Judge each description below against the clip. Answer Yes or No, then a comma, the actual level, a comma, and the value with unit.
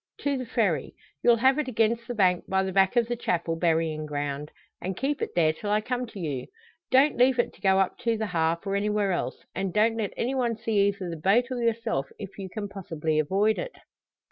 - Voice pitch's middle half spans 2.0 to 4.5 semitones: No, average, 5.1 semitones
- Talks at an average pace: No, fast, 230 wpm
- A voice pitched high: Yes, high, 200 Hz